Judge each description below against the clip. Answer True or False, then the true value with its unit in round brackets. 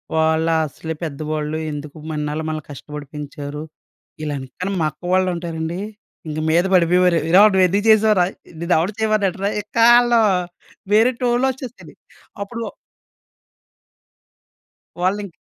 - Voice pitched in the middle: True (175 Hz)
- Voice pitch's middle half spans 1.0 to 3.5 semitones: False (5.1 semitones)